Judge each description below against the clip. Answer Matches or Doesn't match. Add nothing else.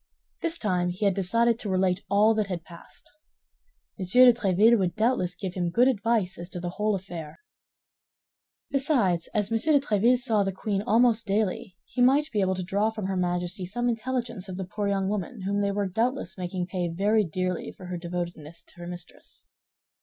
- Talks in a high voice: Matches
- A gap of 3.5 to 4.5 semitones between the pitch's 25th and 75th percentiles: Matches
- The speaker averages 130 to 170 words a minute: Doesn't match